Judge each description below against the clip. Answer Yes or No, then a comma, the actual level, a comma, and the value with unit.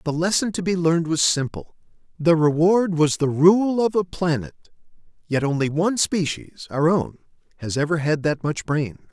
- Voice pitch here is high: No, medium, 165 Hz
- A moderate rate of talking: Yes, average, 180 wpm